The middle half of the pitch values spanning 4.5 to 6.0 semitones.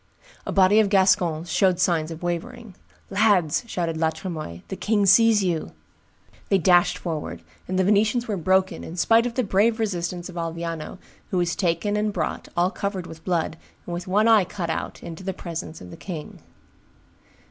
No: average, 3.3 semitones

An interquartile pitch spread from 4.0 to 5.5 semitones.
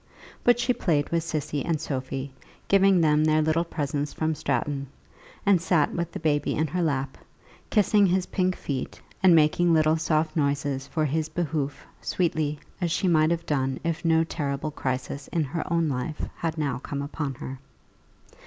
No: average, 2.9 semitones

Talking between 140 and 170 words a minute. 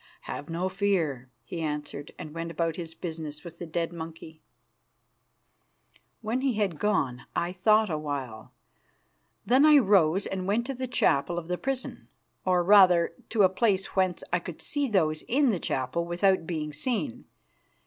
Yes: average, 165 wpm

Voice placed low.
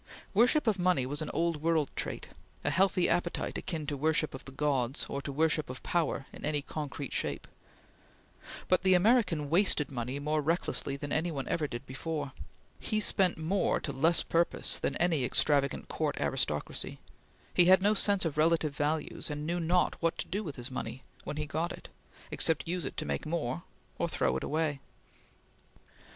No: medium, 155 Hz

